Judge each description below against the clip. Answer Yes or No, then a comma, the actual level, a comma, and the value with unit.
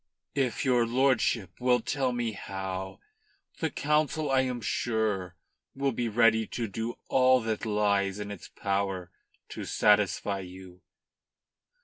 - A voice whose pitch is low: Yes, low, 110 Hz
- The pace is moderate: No, slow, 130 wpm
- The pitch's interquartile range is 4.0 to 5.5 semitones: Yes, average, 4.5 semitones